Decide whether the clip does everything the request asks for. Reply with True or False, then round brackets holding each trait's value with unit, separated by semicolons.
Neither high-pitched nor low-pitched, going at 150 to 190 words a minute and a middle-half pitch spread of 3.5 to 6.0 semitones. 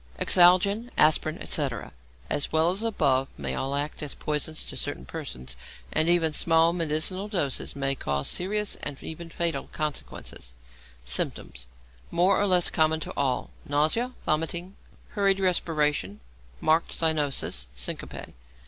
False (155 Hz; 135 wpm; 4.1 semitones)